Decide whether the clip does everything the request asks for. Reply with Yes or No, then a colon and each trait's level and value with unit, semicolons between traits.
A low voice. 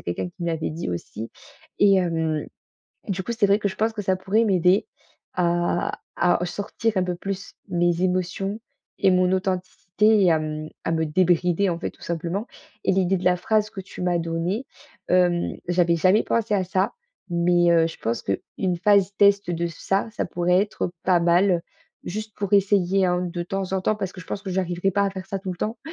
No: medium, 185 Hz